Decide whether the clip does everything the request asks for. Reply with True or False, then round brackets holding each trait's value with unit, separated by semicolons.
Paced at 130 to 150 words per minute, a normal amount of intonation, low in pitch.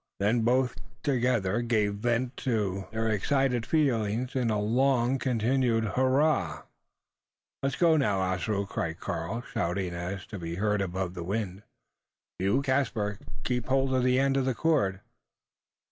True (145 wpm; 4.8 semitones; 115 Hz)